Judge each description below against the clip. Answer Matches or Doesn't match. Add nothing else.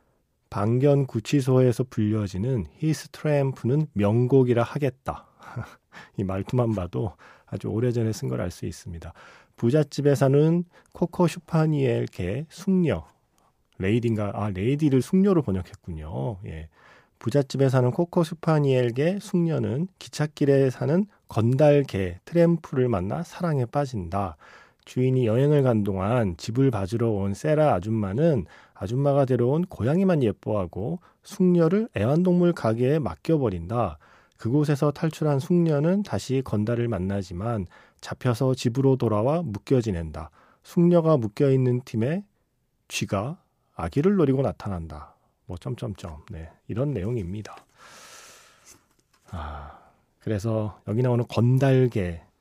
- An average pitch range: Doesn't match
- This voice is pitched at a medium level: Doesn't match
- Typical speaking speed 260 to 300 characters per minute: Matches